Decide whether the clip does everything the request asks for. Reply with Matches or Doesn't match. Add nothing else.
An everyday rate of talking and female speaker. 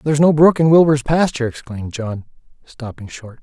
Doesn't match